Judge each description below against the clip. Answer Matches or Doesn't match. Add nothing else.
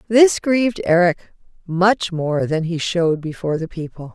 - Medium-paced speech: Matches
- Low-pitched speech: Doesn't match